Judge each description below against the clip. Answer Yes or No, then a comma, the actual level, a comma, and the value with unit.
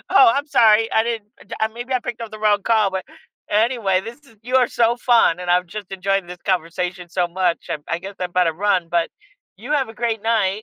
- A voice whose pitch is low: No, high, 210 Hz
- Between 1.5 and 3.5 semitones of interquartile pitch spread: No, average, 4.3 semitones